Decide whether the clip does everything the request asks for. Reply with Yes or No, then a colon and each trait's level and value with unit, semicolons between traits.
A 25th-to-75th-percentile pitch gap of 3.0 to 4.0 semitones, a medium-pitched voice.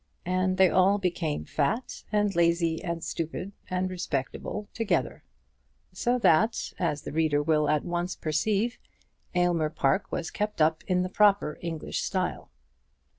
Yes: average, 3.7 semitones; medium, 175 Hz